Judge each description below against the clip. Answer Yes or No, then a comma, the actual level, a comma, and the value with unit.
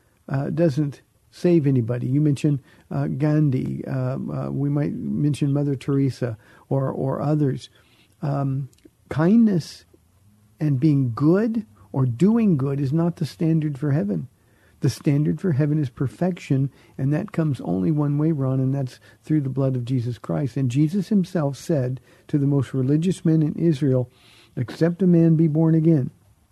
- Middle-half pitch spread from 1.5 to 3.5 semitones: No, average, 3.9 semitones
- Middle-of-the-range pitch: Yes, medium, 145 Hz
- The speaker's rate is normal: Yes, average, 160 wpm